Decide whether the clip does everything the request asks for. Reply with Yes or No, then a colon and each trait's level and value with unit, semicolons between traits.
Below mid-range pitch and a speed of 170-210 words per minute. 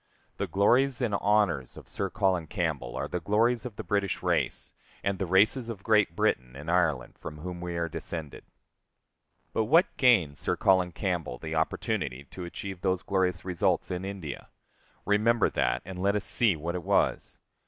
Yes: very low, 95 Hz; average, 175 wpm